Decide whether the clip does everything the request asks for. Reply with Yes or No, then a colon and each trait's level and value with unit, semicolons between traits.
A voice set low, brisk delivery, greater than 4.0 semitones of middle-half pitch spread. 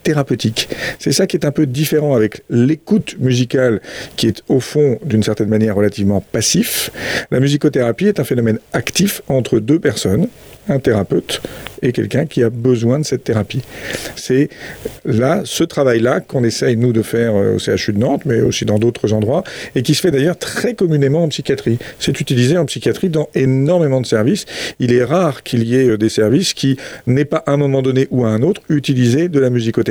No: low, 130 Hz; average, 195 wpm; average, 4.5 semitones